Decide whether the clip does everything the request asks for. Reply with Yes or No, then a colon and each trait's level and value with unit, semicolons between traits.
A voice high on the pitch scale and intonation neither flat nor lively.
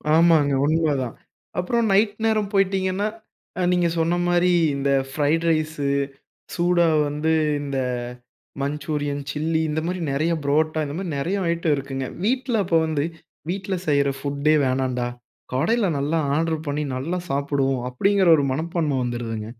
No: medium, 155 Hz; average, 4.0 semitones